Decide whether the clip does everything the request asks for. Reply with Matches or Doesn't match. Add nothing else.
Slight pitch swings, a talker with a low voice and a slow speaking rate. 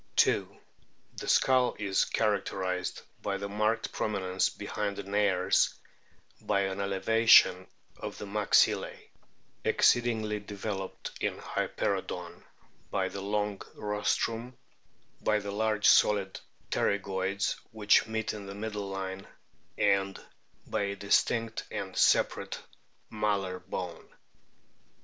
Matches